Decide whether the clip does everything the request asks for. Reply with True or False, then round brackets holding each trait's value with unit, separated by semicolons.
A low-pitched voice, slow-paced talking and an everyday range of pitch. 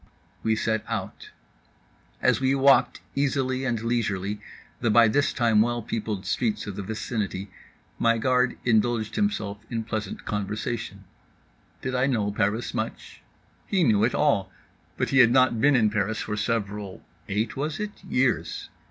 False (115 Hz; 150 wpm; 3.5 semitones)